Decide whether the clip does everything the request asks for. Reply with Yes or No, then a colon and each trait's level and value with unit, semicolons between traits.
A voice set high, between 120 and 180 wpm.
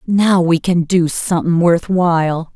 No: medium, 170 Hz; average, 140 wpm